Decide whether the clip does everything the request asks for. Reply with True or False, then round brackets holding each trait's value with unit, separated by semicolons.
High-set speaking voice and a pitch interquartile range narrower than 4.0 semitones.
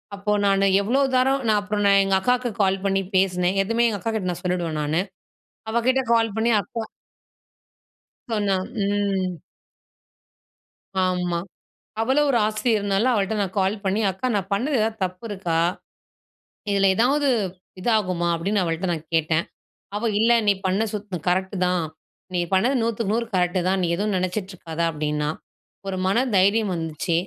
True (195 Hz; 3.3 semitones)